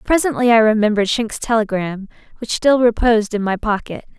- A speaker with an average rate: Yes, average, 160 wpm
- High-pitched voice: Yes, high, 220 Hz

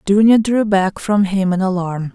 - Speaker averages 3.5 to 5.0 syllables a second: Yes, 4.4 syllables/s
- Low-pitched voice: No, high, 195 Hz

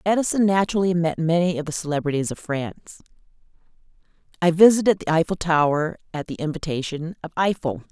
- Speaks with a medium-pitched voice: Yes, medium, 170 Hz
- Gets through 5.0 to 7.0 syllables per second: Yes, 6.1 syllables/s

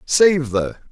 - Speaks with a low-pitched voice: No, medium, 145 Hz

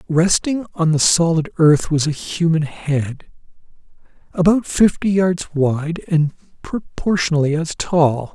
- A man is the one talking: Yes, male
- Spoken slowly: Yes, slow, 120 wpm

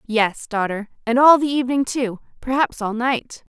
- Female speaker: Yes, female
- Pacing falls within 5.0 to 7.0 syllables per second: No, 4.8 syllables/s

